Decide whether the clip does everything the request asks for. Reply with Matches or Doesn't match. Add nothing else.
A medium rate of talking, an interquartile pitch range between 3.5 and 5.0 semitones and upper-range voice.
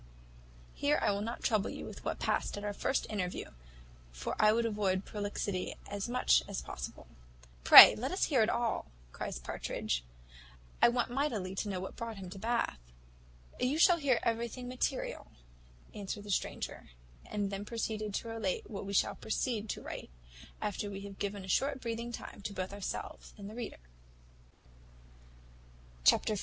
Doesn't match